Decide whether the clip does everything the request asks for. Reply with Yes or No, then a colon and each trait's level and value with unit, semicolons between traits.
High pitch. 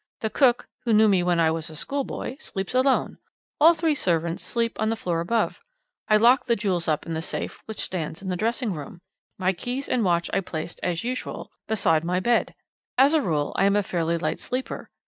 Yes: high, 195 Hz